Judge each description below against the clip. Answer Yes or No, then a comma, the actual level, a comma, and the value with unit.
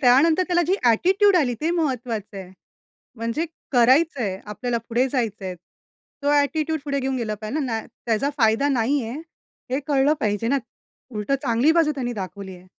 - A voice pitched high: Yes, very high, 250 Hz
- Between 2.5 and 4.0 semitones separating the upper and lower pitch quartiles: No, average, 5.1 semitones